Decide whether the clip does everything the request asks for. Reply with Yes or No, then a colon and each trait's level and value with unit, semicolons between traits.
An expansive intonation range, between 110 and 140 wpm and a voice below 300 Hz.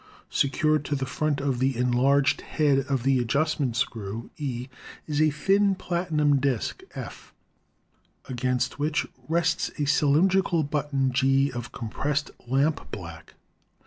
No: average, 3.2 semitones; slow, 135 wpm; medium, 140 Hz